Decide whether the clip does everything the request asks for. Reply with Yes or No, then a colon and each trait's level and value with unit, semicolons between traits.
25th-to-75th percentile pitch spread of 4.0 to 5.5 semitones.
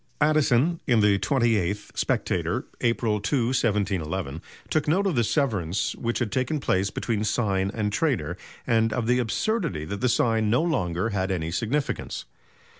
Yes: average, 4.4 semitones